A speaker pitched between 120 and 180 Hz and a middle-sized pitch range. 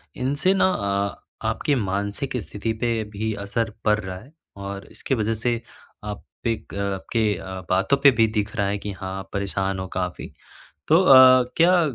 No: low, 105 Hz; average, 4.3 semitones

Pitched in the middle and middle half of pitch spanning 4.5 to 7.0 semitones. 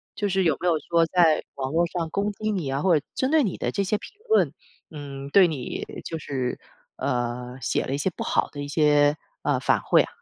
Yes: medium, 160 Hz; average, 5.2 semitones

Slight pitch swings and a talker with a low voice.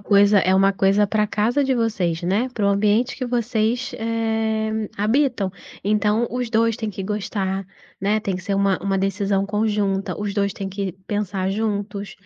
No: narrow, 2.2 semitones; high, 210 Hz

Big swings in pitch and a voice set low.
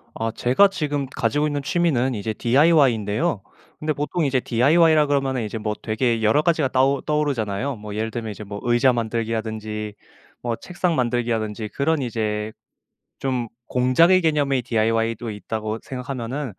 No: average, 4.6 semitones; low, 125 Hz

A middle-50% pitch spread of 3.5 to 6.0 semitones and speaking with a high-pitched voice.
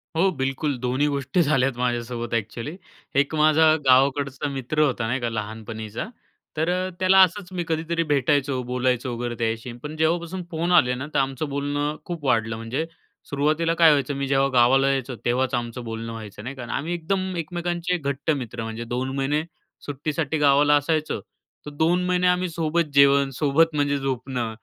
No: average, 4.2 semitones; medium, 140 Hz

